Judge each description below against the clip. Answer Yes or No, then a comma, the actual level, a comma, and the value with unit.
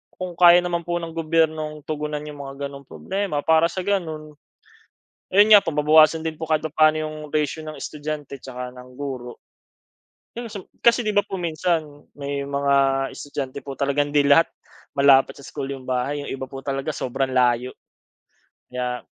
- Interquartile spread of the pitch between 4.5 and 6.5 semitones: No, average, 2.9 semitones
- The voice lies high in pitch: No, medium, 150 Hz